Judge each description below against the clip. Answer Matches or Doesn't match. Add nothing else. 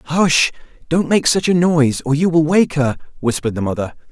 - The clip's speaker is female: Doesn't match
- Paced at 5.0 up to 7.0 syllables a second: Matches